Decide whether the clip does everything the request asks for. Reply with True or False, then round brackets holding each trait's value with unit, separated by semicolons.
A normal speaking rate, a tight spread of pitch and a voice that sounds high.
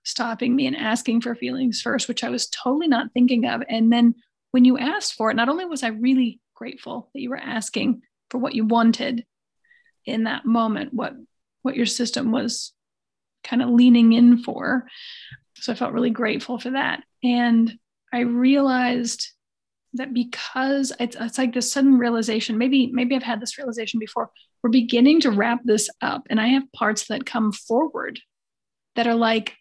True (180 wpm; 2.0 semitones; 245 Hz)